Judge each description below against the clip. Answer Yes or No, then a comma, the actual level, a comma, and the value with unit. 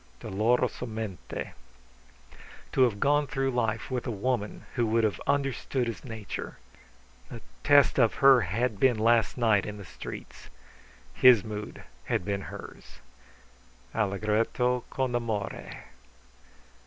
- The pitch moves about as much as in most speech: Yes, average, 3.1 semitones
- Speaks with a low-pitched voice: Yes, low, 115 Hz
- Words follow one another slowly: Yes, slow, 120 wpm